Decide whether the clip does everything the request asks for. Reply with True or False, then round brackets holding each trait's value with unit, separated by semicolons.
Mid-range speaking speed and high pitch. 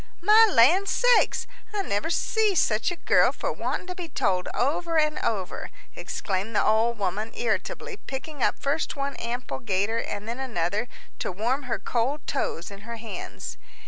True (170 wpm; 240 Hz)